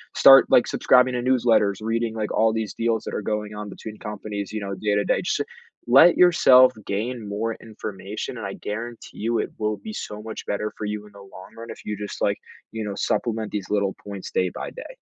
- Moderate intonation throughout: No, narrow, 2.1 semitones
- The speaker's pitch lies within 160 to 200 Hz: No, low, 110 Hz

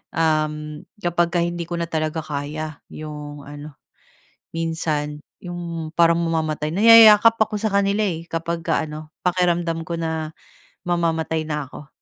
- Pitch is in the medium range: Yes, medium, 165 Hz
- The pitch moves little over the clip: Yes, narrow, 2.0 semitones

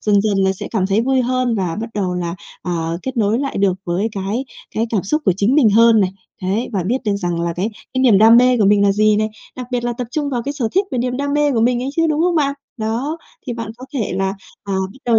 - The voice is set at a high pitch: Yes, high, 225 Hz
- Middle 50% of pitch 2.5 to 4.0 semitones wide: No, average, 4.4 semitones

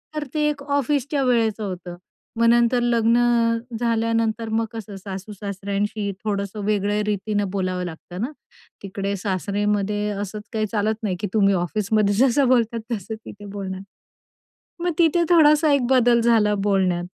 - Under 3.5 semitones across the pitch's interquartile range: Yes, average, 2.9 semitones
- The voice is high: Yes, high, 215 Hz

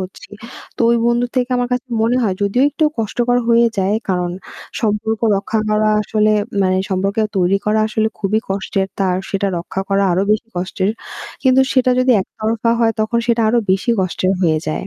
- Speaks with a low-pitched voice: No, high, 215 Hz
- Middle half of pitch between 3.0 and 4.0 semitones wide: Yes, average, 3.6 semitones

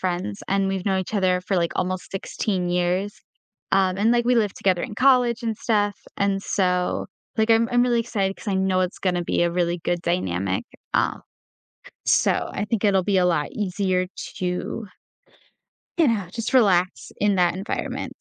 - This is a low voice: No, high, 190 Hz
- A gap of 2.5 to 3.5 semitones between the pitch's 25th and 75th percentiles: Yes, average, 2.9 semitones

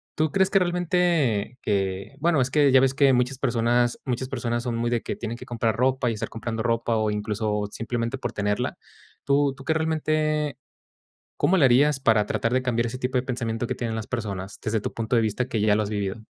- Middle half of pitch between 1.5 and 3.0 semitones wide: No, average, 3.4 semitones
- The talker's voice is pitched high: No, low, 120 Hz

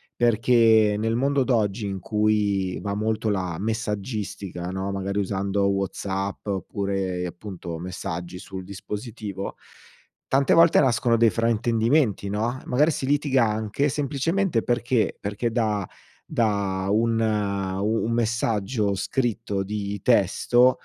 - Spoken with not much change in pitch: No, average, 3.1 semitones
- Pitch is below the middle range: Yes, low, 105 Hz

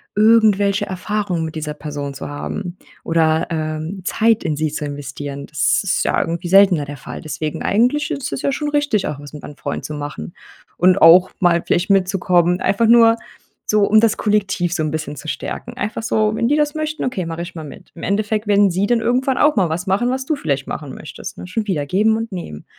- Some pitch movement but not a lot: No, wide, 5.8 semitones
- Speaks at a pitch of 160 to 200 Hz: Yes, medium, 185 Hz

